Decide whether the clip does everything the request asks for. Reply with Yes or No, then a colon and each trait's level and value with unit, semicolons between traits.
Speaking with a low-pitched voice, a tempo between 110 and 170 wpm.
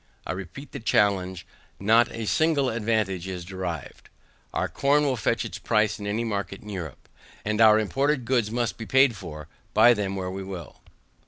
No: low, 105 Hz; average, 180 wpm